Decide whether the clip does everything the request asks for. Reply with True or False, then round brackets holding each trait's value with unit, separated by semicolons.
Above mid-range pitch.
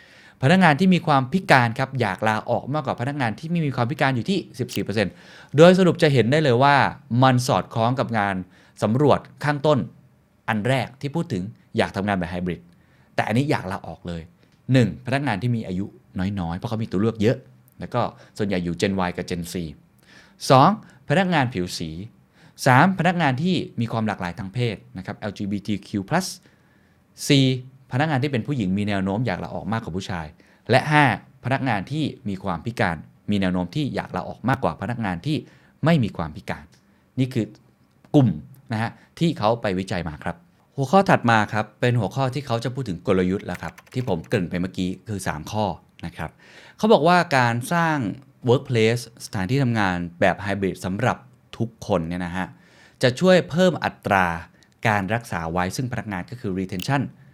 False (110 Hz)